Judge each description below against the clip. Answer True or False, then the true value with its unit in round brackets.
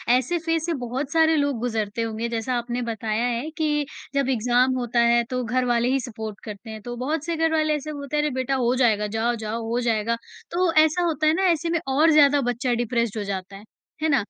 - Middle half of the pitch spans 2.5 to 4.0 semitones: False (4.6 semitones)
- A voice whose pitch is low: False (250 Hz)